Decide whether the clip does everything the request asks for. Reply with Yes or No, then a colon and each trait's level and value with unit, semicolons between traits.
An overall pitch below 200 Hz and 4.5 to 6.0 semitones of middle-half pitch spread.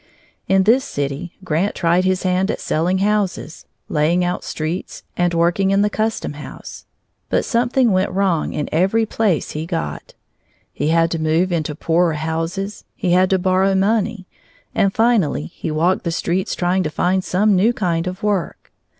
No: medium, 185 Hz; average, 3.0 semitones